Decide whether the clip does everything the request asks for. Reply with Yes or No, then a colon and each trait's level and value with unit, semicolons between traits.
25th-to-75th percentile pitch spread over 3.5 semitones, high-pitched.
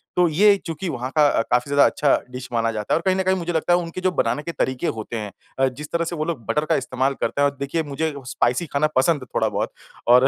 No: average, 4.7 semitones; medium, 145 Hz